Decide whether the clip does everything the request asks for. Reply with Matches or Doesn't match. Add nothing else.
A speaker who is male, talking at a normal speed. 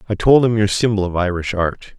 Doesn't match